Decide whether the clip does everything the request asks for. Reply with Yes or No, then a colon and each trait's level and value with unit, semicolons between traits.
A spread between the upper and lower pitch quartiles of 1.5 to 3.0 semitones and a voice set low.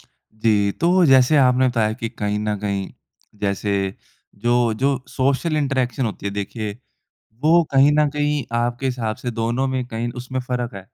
No: average, 3.7 semitones; low, 125 Hz